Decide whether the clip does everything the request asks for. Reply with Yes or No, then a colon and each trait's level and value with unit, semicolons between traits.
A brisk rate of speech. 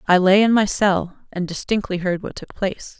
Yes: fast, 220 wpm